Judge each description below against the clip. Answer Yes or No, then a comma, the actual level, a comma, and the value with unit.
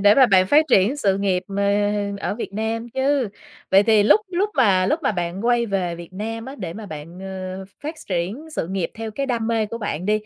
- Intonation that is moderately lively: Yes, average, 4.3 semitones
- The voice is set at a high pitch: Yes, high, 210 Hz